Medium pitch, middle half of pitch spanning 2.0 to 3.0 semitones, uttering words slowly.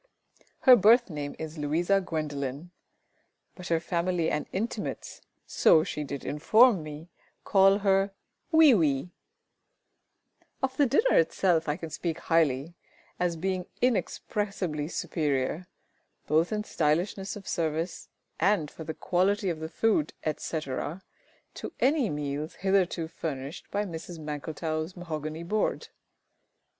No: medium, 170 Hz; average, 4.2 semitones; slow, 125 wpm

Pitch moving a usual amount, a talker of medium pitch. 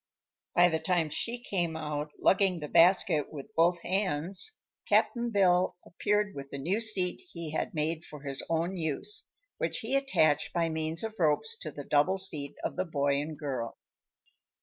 Yes: average, 4.3 semitones; medium, 165 Hz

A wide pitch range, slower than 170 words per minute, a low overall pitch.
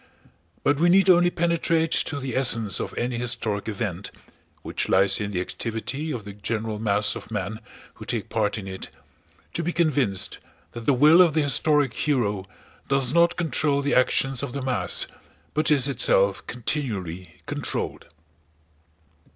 Yes: wide, 6.2 semitones; average, 150 wpm; low, 125 Hz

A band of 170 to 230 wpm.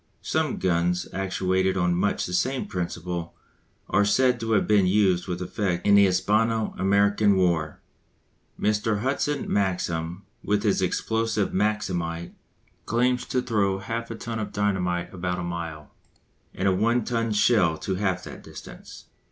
No: average, 150 wpm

